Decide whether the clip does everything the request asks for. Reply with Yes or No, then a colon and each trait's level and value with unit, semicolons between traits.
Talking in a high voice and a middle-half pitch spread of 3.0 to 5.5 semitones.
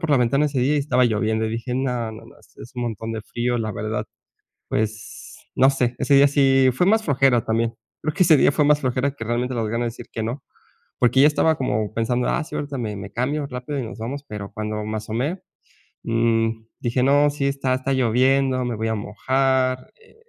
No: low, 125 Hz; average, 3.4 semitones